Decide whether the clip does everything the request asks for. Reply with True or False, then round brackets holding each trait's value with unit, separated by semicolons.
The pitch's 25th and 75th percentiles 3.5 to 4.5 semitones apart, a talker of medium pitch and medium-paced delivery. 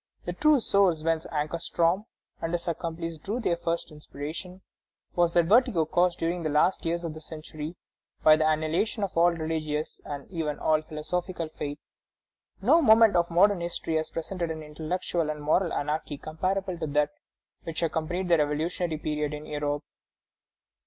False (2.4 semitones; 165 Hz; 160 wpm)